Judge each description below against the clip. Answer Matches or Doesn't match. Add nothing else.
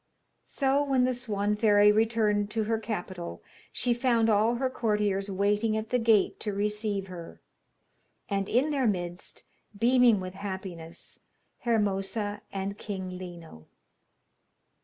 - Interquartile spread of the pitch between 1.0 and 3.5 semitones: Matches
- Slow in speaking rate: Matches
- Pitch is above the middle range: Matches